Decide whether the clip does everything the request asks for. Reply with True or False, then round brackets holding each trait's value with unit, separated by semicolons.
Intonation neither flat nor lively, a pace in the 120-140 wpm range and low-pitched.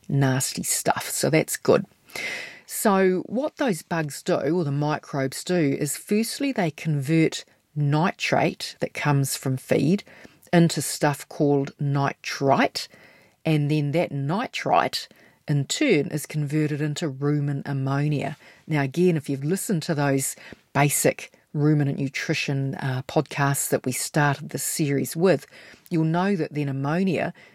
False (3.6 semitones; 135 wpm; 150 Hz)